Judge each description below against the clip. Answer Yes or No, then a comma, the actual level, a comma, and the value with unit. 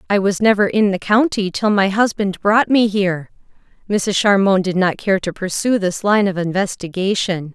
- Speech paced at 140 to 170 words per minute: No, average, 185 wpm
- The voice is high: Yes, high, 195 Hz